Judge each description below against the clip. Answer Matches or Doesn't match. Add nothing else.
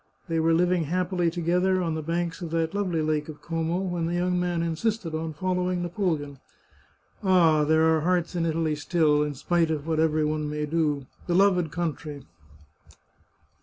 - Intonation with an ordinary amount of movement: Doesn't match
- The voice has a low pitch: Doesn't match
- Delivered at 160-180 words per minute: Matches